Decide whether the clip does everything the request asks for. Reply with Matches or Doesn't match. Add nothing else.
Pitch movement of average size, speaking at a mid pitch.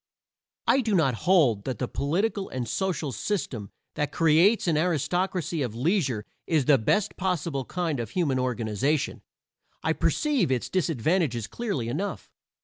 Doesn't match